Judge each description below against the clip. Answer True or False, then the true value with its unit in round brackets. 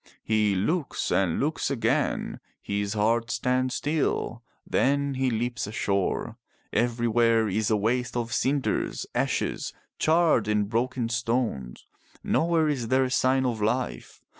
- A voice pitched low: True (120 Hz)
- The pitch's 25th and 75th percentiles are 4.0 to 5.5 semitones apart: False (3.2 semitones)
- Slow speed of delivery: True (130 wpm)